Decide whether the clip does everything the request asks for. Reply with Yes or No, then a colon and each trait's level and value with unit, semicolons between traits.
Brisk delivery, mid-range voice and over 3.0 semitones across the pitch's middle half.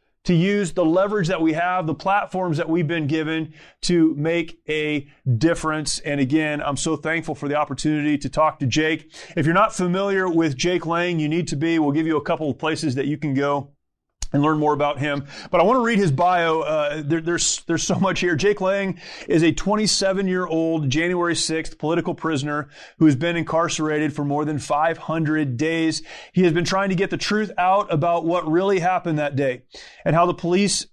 No: fast, 210 wpm; medium, 160 Hz; narrow, 2.5 semitones